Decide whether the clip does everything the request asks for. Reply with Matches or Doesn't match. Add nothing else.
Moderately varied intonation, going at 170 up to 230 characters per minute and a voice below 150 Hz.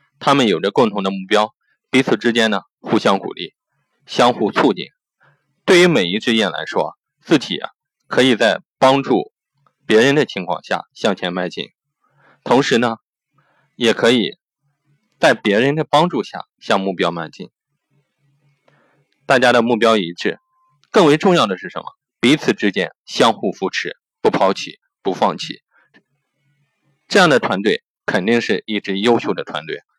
Matches